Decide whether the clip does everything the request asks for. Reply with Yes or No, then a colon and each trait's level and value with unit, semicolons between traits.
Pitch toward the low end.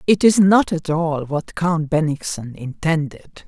No: medium, 160 Hz